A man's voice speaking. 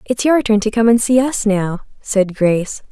No: female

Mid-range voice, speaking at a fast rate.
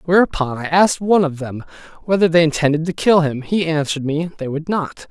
Yes: medium, 160 Hz; fast, 210 wpm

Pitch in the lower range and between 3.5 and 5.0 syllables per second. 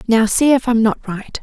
No: high, 230 Hz; 4.7 syllables/s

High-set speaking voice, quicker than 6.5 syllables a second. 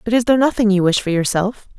Yes: high, 210 Hz; 6.8 syllables/s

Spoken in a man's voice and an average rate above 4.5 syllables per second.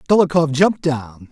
Yes: male; 5.5 syllables/s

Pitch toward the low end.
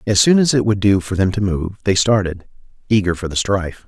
Yes: low, 100 Hz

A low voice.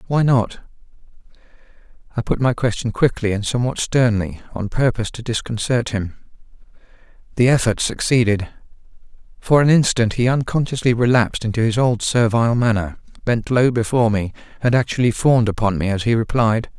Yes: low, 115 Hz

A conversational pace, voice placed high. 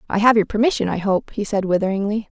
No: fast, 225 wpm; high, 205 Hz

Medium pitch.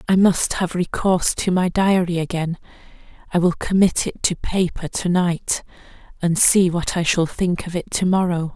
Yes: medium, 175 Hz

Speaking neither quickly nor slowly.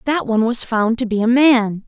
No: fast, 255 wpm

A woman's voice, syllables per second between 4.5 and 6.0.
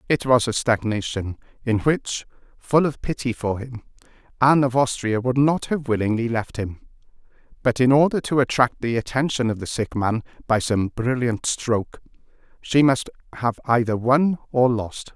No: male; 4.8 syllables/s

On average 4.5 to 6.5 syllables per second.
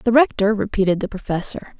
Yes: 5.8 syllables/s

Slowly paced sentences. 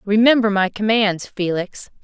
Yes: slow, 120 wpm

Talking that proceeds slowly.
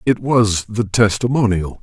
Yes: slow, 130 wpm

